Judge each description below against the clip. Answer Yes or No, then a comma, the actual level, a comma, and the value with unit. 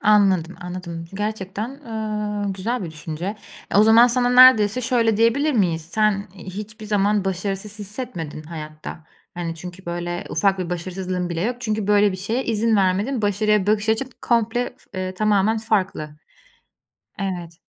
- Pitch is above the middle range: Yes, high, 205 Hz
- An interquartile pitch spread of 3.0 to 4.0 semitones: Yes, average, 3.4 semitones